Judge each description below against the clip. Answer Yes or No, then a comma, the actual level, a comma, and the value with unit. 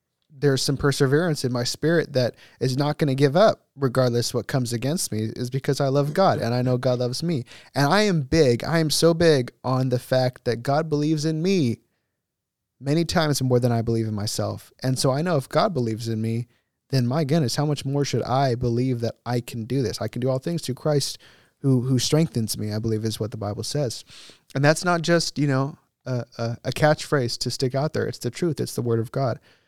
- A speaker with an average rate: No, fast, 235 wpm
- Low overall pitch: Yes, low, 130 Hz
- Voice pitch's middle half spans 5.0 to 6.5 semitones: No, average, 3.8 semitones